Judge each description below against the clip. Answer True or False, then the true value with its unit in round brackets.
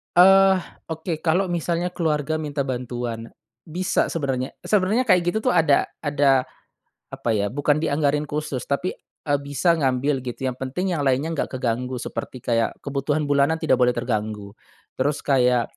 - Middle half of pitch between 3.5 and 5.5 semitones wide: True (4.1 semitones)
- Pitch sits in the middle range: True (145 Hz)